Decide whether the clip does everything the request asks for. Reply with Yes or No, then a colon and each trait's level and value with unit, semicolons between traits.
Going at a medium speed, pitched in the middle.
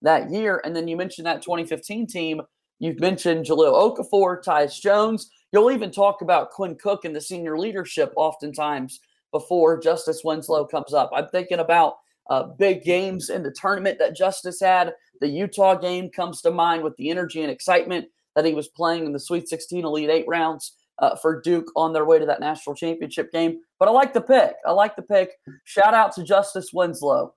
Yes: average, 195 wpm; medium, 170 Hz